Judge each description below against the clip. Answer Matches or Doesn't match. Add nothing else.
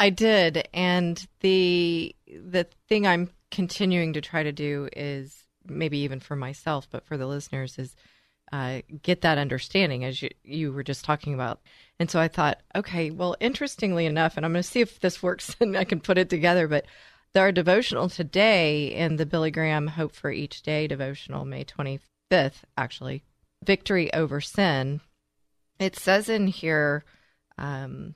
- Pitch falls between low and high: Matches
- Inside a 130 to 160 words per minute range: Doesn't match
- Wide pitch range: Doesn't match